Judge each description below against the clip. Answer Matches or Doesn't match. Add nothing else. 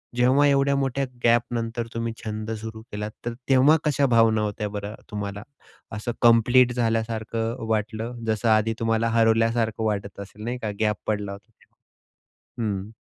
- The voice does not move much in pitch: Matches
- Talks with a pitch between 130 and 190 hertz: Doesn't match